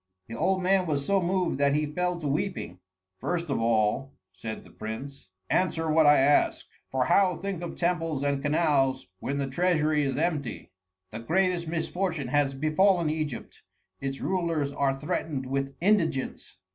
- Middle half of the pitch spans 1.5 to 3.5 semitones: No, average, 4.3 semitones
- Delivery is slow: No, average, 160 wpm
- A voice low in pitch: No, medium, 150 Hz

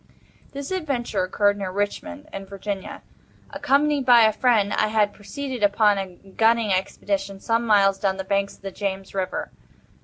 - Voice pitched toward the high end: Yes, high, 205 Hz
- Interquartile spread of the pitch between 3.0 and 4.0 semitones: Yes, average, 3.3 semitones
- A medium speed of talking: Yes, average, 160 wpm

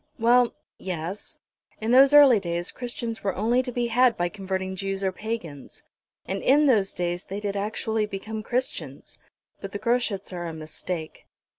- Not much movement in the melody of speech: No, average, 4.2 semitones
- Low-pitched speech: No, high, 205 Hz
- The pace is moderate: Yes, average, 165 wpm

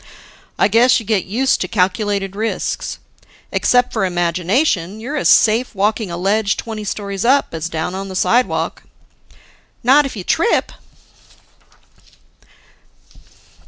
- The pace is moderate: No, slow, 125 wpm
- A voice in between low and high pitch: No, high, 210 Hz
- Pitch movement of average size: Yes, average, 3.9 semitones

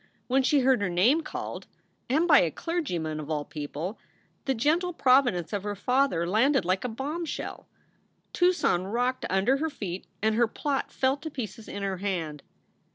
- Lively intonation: Yes, wide, 7.2 semitones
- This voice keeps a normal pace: Yes, average, 170 wpm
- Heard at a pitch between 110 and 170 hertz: No, high, 235 Hz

